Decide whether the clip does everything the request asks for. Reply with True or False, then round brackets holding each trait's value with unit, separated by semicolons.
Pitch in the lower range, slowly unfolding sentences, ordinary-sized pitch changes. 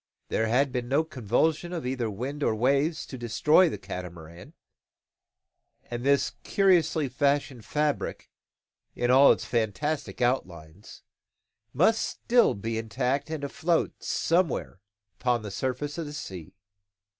True (130 Hz; 130 wpm; 5.0 semitones)